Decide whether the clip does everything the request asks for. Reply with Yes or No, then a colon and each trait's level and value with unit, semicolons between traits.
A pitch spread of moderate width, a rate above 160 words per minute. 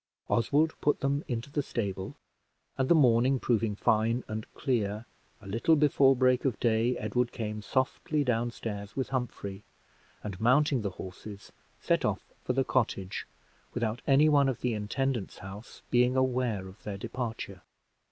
No: average, 3.7 semitones; average, 155 wpm